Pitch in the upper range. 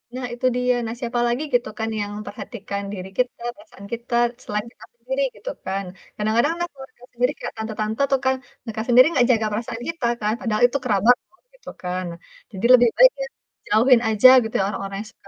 Yes: high, 235 Hz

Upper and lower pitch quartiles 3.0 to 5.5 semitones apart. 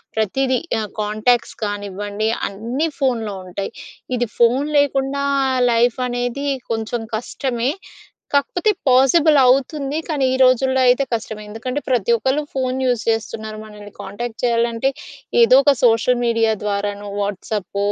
Yes: average, 3.6 semitones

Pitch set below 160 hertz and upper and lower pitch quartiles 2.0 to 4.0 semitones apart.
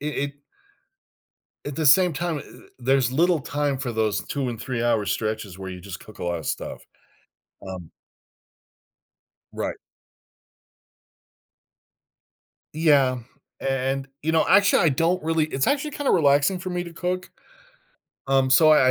No: medium, 140 Hz; wide, 5.5 semitones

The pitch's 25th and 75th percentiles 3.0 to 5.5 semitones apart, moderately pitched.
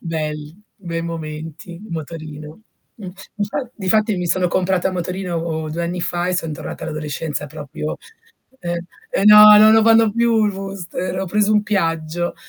Yes: average, 4.0 semitones; medium, 175 Hz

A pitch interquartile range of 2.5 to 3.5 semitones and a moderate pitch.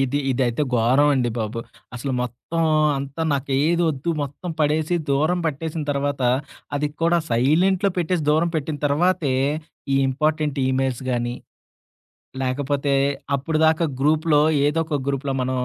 Yes: average, 3.0 semitones; medium, 145 Hz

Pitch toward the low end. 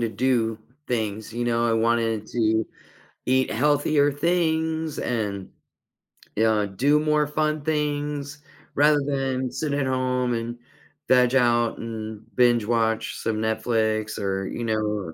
Yes: low, 120 Hz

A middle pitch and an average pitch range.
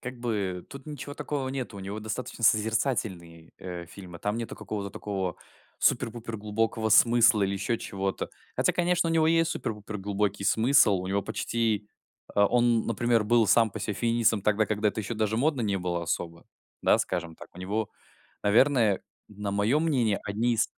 No: low, 110 Hz; average, 3.2 semitones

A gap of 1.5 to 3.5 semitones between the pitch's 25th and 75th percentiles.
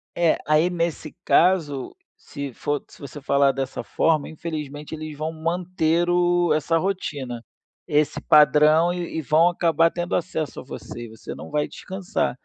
Yes: average, 2.9 semitones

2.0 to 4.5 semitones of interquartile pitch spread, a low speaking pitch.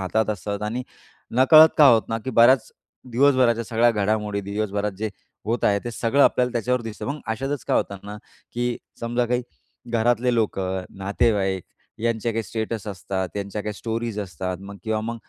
Yes: average, 2.7 semitones; low, 110 Hz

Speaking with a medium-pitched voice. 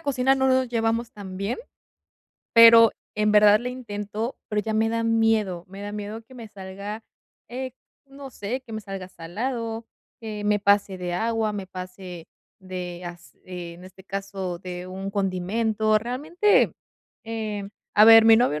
No: high, 210 Hz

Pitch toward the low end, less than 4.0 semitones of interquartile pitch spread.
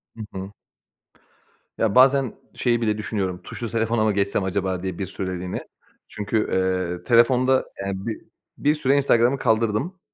No: low, 110 Hz; average, 4.4 semitones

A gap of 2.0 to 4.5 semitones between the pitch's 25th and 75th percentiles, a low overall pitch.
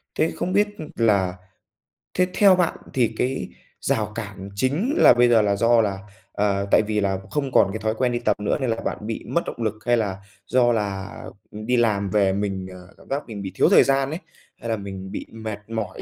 Yes: average, 3.9 semitones; low, 110 Hz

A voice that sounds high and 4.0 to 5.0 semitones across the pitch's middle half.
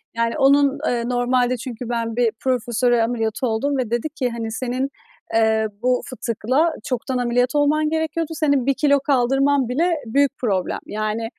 No: very high, 250 Hz; average, 3.2 semitones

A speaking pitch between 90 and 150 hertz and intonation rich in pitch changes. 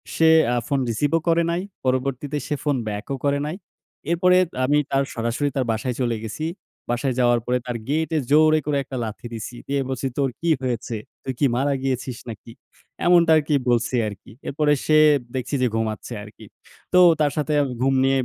No: low, 135 Hz; average, 3.6 semitones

